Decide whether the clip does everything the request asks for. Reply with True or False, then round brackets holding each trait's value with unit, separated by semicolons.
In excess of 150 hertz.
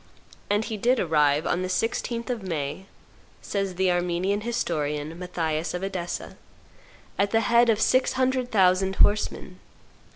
True (190 Hz)